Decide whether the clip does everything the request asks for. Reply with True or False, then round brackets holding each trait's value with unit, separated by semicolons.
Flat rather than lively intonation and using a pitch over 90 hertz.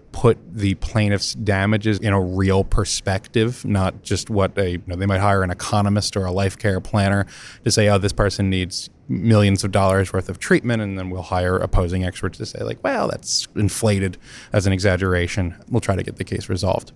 True (1.9 semitones; 100 Hz)